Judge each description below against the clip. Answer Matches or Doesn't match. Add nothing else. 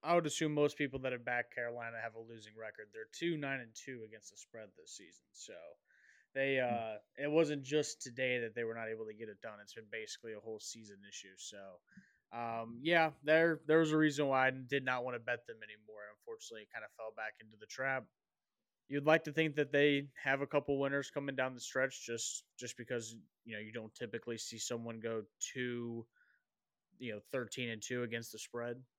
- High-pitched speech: Doesn't match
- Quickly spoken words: Matches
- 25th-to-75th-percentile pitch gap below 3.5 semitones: Doesn't match